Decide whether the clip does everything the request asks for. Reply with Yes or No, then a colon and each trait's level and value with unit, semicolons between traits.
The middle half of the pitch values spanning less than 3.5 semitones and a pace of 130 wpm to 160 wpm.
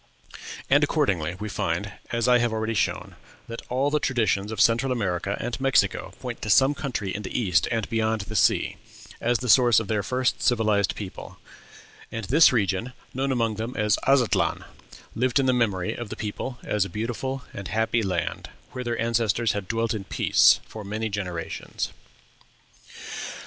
No: average, 3.1 semitones; average, 175 wpm